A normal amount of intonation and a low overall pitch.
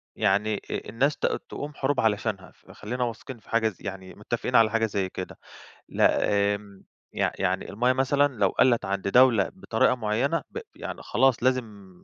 Yes: average, 4.0 semitones; low, 110 Hz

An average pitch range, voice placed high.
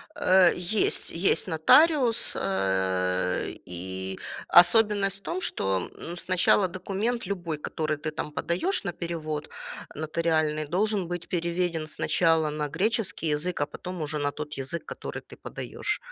No: average, 4.1 semitones; medium, 170 Hz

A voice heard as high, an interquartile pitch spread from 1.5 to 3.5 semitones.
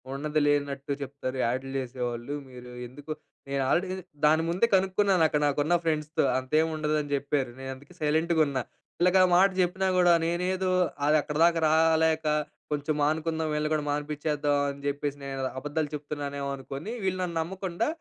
No: medium, 150 Hz; average, 3.0 semitones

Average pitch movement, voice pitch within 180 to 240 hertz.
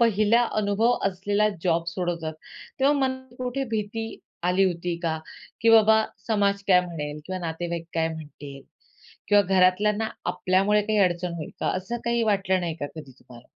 Yes: average, 4.2 semitones; high, 190 Hz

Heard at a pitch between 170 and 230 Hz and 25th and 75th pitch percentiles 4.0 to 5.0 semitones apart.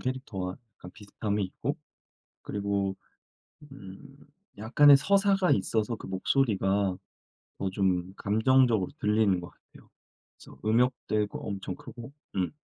No: low, 105 Hz; average, 4.7 semitones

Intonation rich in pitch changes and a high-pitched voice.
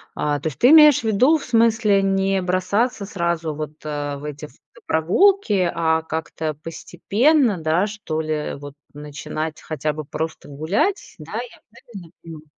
No: wide, 5.7 semitones; medium, 170 Hz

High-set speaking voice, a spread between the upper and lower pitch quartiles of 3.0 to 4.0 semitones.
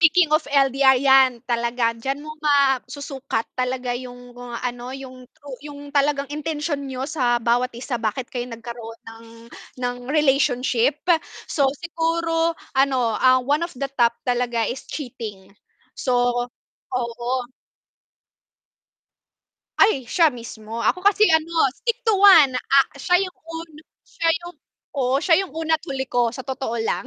Yes: very high, 265 Hz; average, 3.6 semitones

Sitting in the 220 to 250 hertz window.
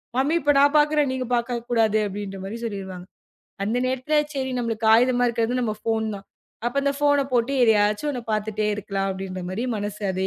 Yes: high, 230 Hz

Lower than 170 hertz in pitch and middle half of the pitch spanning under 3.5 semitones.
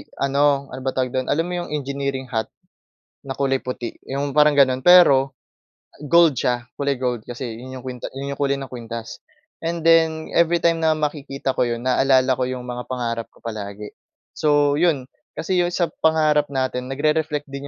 Yes: low, 135 Hz; average, 3.0 semitones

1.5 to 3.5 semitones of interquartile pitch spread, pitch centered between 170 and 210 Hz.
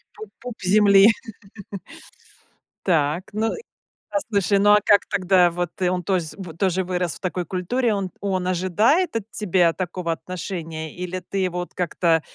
Yes: narrow, 2.4 semitones; medium, 185 Hz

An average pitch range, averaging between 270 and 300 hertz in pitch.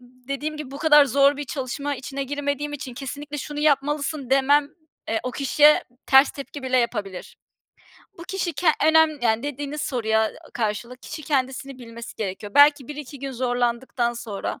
Yes: average, 3.1 semitones; very high, 275 Hz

